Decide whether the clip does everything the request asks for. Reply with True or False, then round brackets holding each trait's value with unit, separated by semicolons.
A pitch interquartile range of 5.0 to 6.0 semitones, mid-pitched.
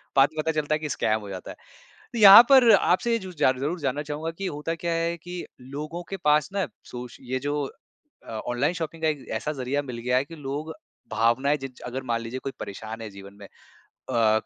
True (5.5 semitones; 145 Hz)